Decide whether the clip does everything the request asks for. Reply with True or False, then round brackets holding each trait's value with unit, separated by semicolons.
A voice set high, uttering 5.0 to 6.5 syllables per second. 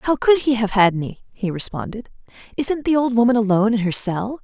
True (230 Hz; 5.8 syllables/s)